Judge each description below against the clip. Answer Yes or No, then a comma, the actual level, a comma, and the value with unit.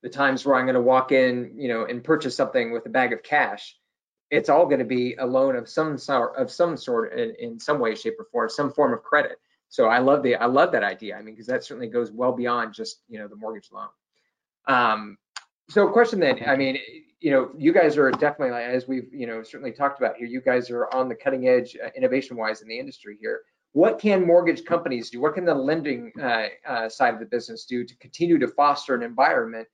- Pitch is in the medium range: No, low, 130 Hz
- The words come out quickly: Yes, fast, 240 wpm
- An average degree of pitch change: No, wide, 6.1 semitones